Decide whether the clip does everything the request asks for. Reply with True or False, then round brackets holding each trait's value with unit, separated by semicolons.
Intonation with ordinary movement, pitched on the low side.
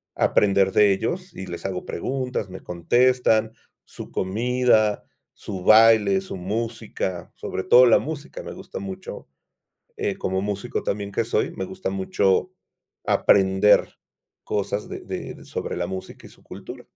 True (4.2 semitones; 105 Hz)